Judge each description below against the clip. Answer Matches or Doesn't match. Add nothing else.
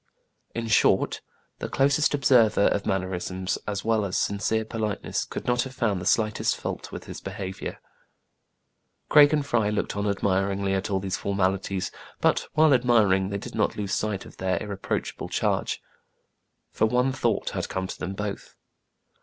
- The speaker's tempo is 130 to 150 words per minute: Doesn't match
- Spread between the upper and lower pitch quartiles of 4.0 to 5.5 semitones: Doesn't match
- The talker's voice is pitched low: Matches